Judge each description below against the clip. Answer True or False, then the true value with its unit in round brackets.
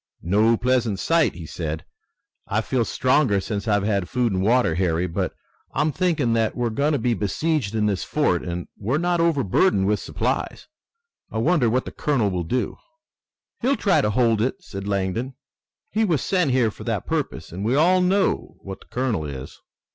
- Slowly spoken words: False (185 wpm)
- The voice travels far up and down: True (6.6 semitones)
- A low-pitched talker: True (115 Hz)